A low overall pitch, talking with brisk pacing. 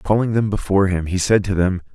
Yes: very low, 95 Hz; fast, 245 wpm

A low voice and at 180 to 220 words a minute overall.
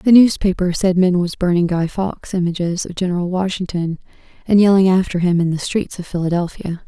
No: medium, 180 Hz; average, 185 wpm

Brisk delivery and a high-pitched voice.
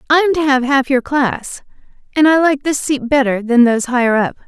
Yes: fast, 230 wpm; very high, 270 Hz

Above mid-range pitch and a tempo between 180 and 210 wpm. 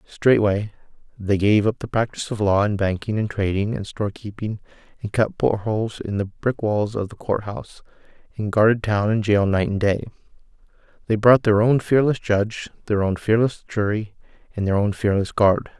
No: low, 105 Hz; average, 190 wpm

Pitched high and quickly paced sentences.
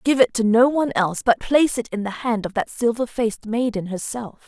Yes: high, 230 Hz; fast, 240 wpm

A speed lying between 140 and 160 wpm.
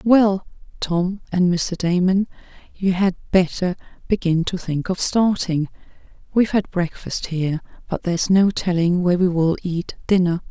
Yes: average, 150 wpm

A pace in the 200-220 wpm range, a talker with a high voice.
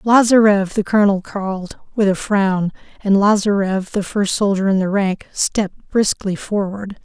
No: average, 155 wpm; high, 200 Hz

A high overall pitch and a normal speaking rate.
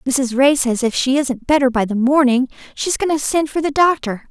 No: very high, 270 Hz; fast, 235 wpm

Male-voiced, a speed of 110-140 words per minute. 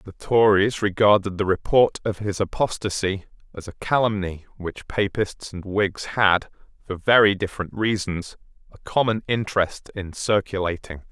Yes: male; slow, 135 wpm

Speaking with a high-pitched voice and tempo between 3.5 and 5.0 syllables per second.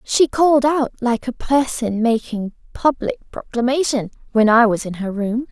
Yes: high, 245 Hz; 4.5 syllables/s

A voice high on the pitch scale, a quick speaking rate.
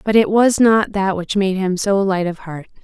Yes: high, 195 Hz; fast, 255 wpm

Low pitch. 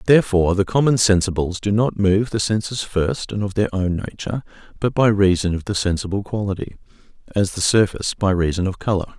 Yes: low, 100 Hz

